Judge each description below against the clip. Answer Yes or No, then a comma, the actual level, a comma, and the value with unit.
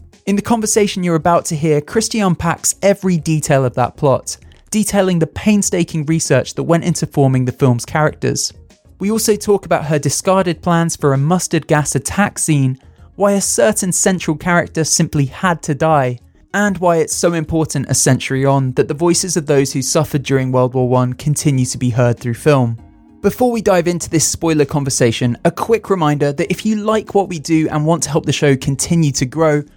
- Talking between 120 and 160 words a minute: No, average, 200 wpm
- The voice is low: No, medium, 160 Hz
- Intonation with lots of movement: No, average, 4.8 semitones